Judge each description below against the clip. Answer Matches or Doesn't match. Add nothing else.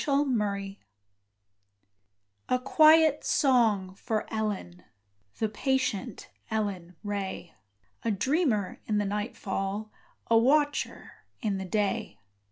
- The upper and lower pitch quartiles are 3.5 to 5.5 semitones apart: Matches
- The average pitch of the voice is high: Matches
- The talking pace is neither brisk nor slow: Doesn't match